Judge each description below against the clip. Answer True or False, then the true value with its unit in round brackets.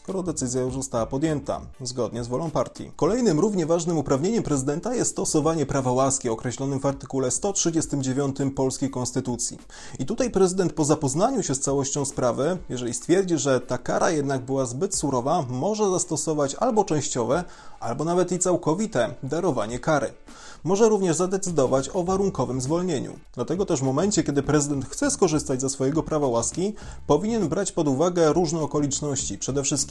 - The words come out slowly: False (155 wpm)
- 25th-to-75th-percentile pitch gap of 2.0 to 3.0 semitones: False (4.9 semitones)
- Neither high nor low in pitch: True (145 Hz)